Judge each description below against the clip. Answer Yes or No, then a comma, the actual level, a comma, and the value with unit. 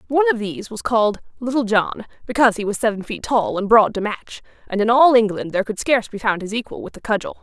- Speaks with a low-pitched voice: No, high, 225 Hz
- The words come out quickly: Yes, fast, 250 wpm